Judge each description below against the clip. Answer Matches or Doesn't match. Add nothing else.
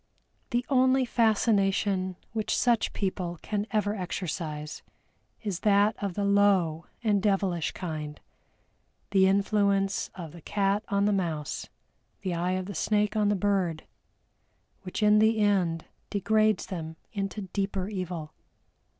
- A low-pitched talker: Doesn't match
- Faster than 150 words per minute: Doesn't match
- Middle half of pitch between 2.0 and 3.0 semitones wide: Matches